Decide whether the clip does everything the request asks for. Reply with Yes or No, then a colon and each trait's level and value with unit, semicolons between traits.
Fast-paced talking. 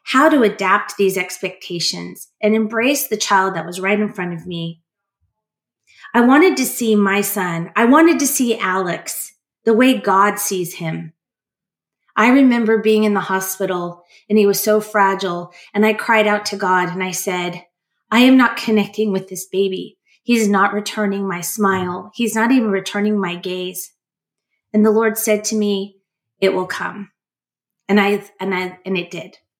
No: average, 175 wpm